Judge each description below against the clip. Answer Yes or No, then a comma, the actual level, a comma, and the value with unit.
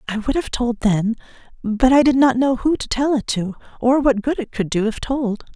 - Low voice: No, high, 245 Hz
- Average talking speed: No, fast, 250 wpm